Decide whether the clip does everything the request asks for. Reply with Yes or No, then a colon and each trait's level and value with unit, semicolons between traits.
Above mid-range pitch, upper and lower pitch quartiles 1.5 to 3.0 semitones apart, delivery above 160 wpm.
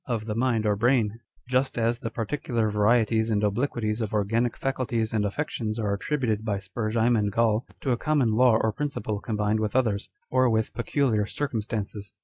No: low, 110 Hz; narrow, 2.4 semitones; average, 175 wpm